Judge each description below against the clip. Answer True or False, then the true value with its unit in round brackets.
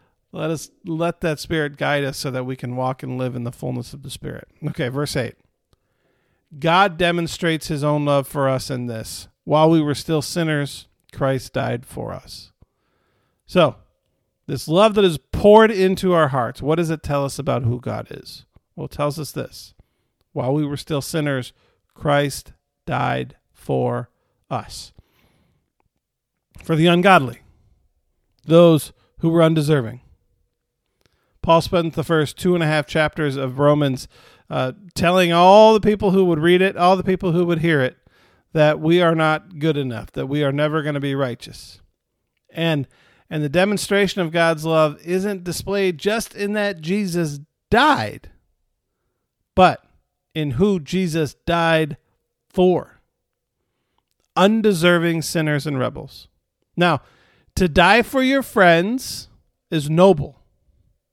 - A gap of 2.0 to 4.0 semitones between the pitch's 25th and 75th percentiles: False (4.6 semitones)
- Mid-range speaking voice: True (155 Hz)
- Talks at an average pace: True (150 wpm)